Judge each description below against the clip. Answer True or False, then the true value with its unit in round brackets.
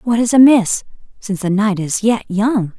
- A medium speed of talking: True (195 wpm)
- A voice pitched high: True (210 Hz)